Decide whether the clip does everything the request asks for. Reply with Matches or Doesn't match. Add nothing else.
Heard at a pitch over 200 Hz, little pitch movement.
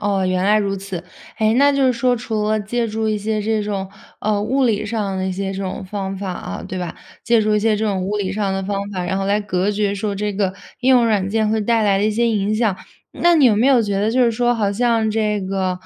Matches